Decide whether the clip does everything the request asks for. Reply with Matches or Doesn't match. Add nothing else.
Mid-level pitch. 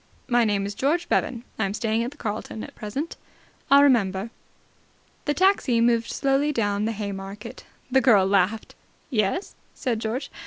Doesn't match